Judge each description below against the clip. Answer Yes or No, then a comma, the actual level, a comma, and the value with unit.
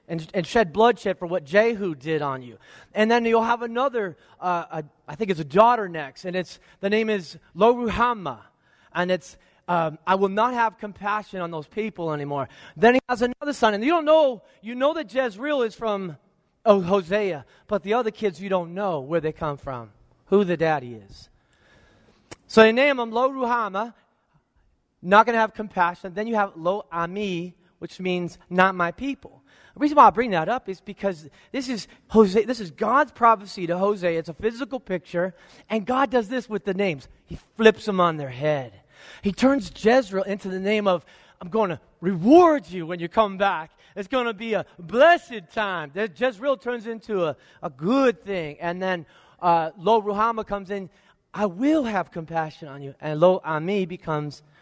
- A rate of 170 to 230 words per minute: Yes, average, 190 wpm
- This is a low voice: No, high, 200 Hz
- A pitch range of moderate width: Yes, average, 5.0 semitones